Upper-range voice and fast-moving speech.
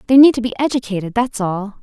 Yes: high, 230 Hz; fast, 230 wpm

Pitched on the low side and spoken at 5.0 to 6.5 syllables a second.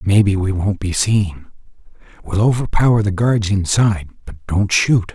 No: low, 100 Hz; 4.7 syllables/s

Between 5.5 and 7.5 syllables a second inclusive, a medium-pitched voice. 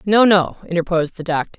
Yes: 6.4 syllables/s; medium, 180 Hz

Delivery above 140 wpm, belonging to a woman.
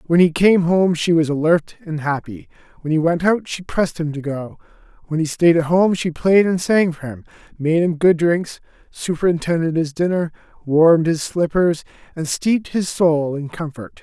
No: average, 190 wpm; male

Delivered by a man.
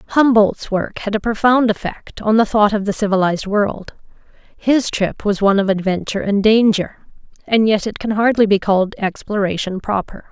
No: female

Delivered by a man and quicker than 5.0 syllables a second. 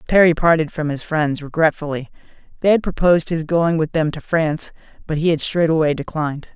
Yes: male; 5.7 syllables/s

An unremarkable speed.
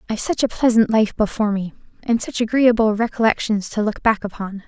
Yes: average, 190 wpm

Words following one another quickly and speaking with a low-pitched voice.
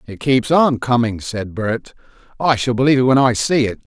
No: average, 195 wpm; low, 125 Hz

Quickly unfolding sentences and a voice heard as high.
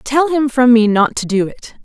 Yes: fast, 260 wpm; very high, 250 Hz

